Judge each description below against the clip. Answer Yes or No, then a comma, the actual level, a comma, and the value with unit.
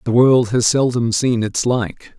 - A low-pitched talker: Yes, low, 120 Hz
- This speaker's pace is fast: No, average, 190 wpm